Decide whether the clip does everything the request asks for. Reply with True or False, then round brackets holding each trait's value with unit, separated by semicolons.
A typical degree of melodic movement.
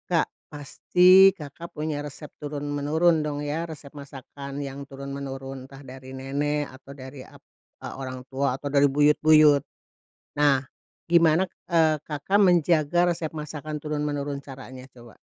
False (2.2 semitones)